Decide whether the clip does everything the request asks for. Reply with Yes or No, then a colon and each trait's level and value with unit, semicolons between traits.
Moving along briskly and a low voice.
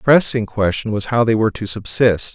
Yes: fast, 230 wpm; low, 110 Hz